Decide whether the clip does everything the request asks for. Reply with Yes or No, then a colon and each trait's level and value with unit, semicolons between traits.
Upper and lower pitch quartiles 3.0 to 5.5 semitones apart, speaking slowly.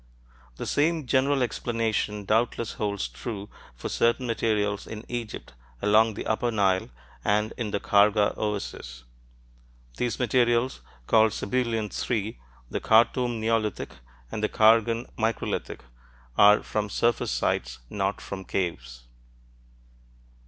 No: narrow, 2.4 semitones; slow, 115 wpm